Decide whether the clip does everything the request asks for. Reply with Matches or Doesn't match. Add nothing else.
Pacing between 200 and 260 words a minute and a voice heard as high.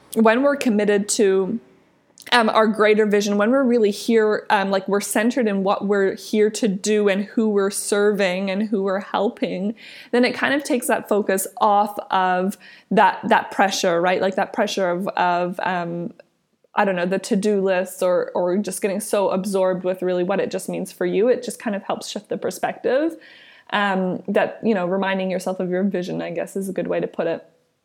Matches